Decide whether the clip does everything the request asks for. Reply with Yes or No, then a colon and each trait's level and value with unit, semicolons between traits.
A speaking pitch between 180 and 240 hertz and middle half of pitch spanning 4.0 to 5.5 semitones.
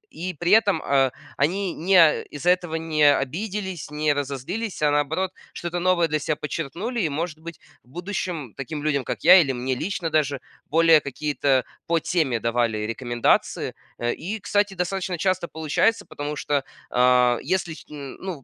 No: medium, 160 Hz; average, 4.4 semitones